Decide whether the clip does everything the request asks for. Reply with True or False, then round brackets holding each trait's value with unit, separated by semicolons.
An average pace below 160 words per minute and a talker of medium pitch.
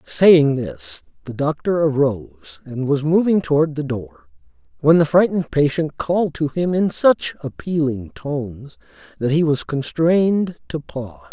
True (150 wpm; 150 Hz)